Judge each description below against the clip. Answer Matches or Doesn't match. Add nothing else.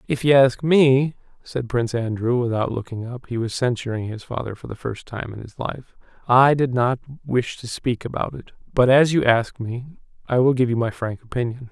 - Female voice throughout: Doesn't match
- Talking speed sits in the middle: Doesn't match